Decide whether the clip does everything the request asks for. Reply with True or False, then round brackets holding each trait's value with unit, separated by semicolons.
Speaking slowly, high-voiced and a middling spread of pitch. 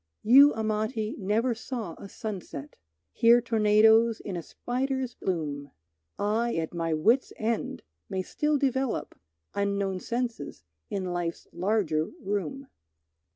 True (115 wpm; 215 Hz; 4.3 semitones)